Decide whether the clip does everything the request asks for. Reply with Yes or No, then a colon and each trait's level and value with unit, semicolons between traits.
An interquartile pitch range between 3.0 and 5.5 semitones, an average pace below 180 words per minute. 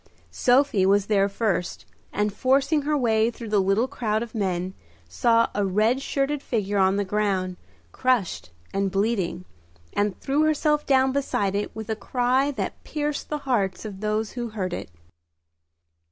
Yes: average, 4.9 semitones; average, 160 wpm